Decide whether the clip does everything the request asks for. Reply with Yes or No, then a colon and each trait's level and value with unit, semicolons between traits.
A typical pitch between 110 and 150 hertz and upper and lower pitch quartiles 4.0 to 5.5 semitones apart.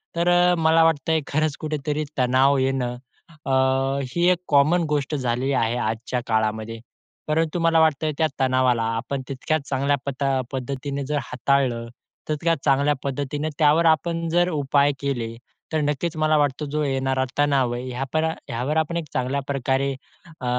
No: medium, 140 Hz; average, 3.2 semitones